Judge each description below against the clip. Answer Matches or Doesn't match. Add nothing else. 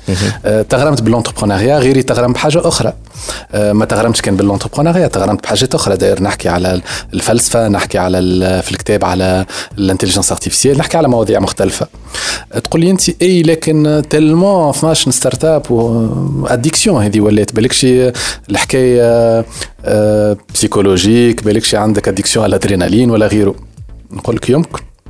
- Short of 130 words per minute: Doesn't match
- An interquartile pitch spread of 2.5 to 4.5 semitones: Doesn't match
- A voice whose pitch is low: Matches